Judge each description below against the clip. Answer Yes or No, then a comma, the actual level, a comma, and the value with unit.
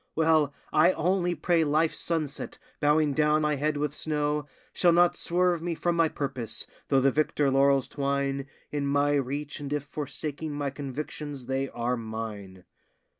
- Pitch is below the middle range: No, medium, 145 Hz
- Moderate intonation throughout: No, narrow, 2.2 semitones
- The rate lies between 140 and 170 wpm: Yes, average, 160 wpm